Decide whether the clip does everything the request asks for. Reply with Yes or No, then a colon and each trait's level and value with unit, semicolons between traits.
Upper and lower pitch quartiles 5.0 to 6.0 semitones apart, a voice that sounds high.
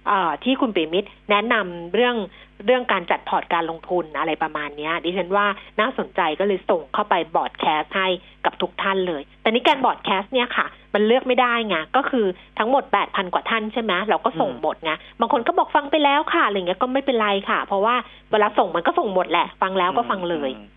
Yes: wide, 5.4 semitones; high, 205 Hz